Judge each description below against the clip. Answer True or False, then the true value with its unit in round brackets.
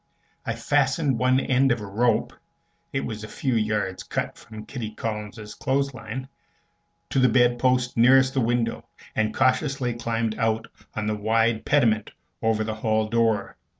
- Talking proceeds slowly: False (155 wpm)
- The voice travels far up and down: False (2.9 semitones)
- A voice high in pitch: False (115 Hz)